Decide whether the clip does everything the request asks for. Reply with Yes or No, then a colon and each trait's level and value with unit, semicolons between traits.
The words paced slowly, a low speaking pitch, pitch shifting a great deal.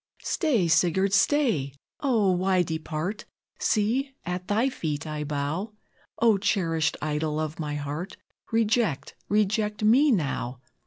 No: slow, 120 wpm; medium, 185 Hz; wide, 5.9 semitones